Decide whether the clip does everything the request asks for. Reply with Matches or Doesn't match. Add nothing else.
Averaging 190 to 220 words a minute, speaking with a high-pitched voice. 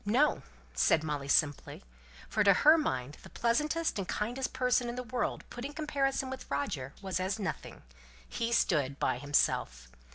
Doesn't match